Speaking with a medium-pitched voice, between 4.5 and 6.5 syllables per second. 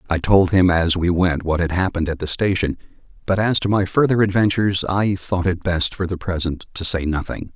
No: very low, 90 Hz; 5.4 syllables/s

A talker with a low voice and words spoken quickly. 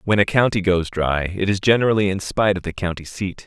Yes: very low, 95 Hz; fast, 240 wpm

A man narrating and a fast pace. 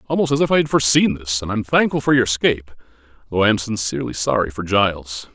Yes: male; fast, 260 wpm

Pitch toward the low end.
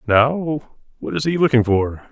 Yes: low, 130 Hz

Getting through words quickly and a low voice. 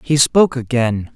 No: average, 155 wpm; low, 130 Hz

